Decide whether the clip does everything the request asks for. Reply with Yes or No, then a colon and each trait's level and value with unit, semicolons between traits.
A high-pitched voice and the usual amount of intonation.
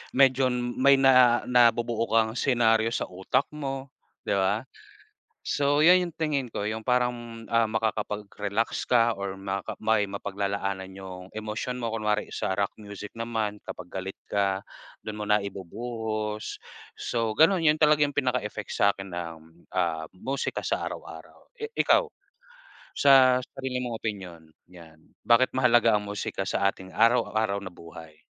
No: low, 110 Hz; average, 4.0 semitones